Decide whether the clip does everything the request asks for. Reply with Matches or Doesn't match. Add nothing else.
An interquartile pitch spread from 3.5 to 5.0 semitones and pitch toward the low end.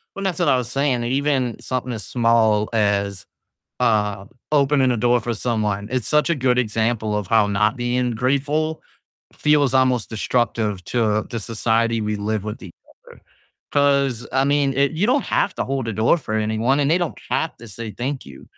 Matches